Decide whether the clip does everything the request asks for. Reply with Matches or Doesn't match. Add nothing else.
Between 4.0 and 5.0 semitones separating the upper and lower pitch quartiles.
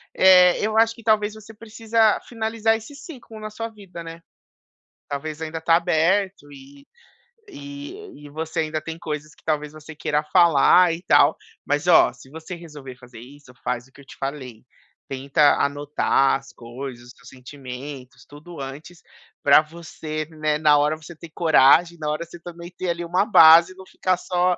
Matches